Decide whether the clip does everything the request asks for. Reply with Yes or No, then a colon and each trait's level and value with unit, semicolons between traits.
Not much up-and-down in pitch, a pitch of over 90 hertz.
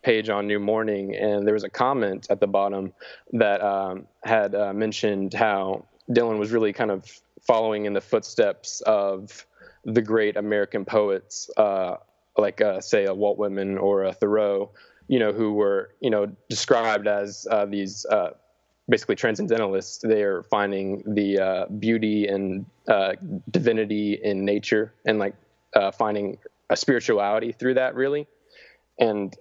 Yes: narrow, 1.5 semitones; low, 105 Hz